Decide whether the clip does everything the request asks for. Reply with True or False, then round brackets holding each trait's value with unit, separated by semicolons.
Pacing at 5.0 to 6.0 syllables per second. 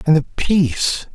False (4.5 syllables/s)